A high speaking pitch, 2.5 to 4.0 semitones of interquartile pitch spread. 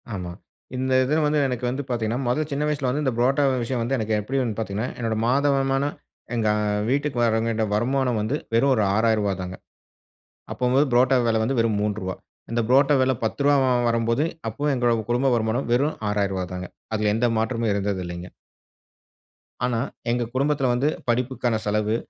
No: low, 120 Hz; average, 3.6 semitones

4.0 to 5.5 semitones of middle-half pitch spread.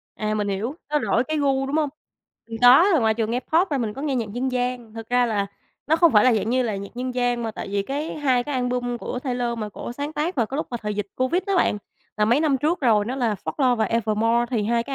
No: average, 3.6 semitones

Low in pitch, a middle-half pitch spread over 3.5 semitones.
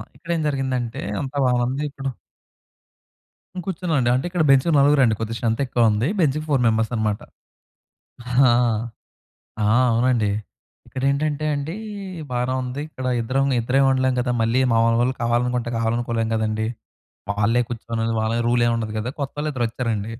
No: low, 125 Hz; average, 3.1 semitones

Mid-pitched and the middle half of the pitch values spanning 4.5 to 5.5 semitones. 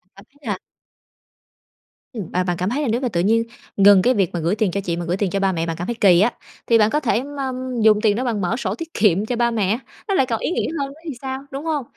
No: high, 215 Hz; average, 5.2 semitones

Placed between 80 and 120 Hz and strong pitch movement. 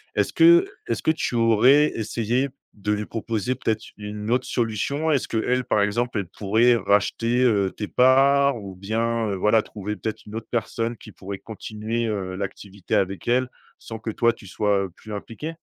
No: low, 110 Hz; average, 3.0 semitones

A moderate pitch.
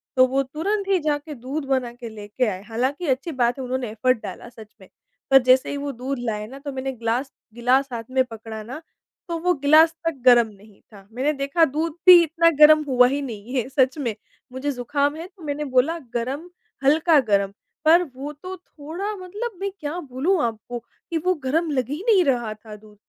No: very high, 270 Hz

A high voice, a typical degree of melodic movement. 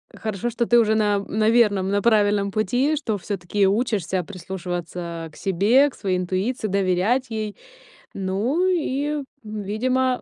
Yes: high, 210 Hz; average, 4.0 semitones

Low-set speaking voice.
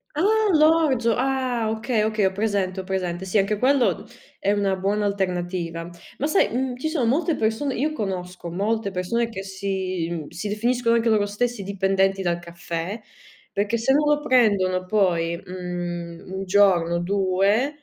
No: high, 200 Hz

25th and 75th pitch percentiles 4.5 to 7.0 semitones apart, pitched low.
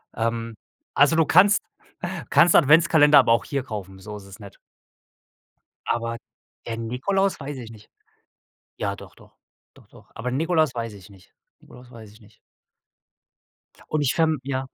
Yes: average, 5.3 semitones; low, 125 Hz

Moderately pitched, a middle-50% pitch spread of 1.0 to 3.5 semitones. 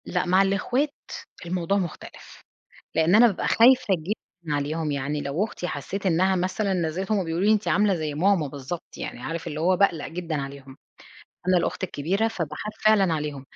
No: medium, 175 Hz; average, 4.3 semitones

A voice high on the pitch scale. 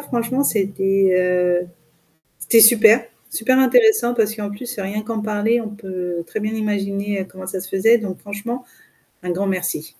Yes: high, 210 Hz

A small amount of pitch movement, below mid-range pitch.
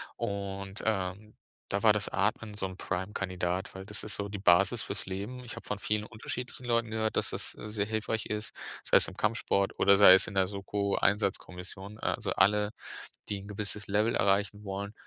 Yes: narrow, 1.7 semitones; low, 100 Hz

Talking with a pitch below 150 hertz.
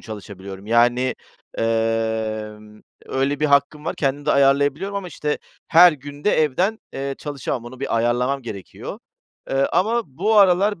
Yes: low, 135 Hz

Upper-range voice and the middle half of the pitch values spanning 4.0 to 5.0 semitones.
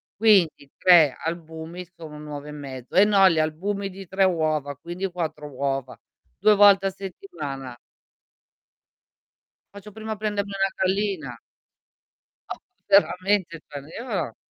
No: medium, 175 Hz; average, 4.7 semitones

